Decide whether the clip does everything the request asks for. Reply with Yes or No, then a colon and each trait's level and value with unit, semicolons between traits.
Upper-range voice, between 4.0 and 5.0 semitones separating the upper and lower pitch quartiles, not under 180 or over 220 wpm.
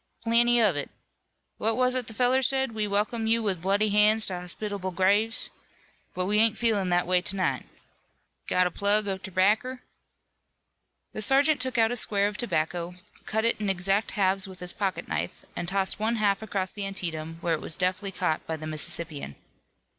No: high, 200 Hz; average, 3.5 semitones; average, 190 wpm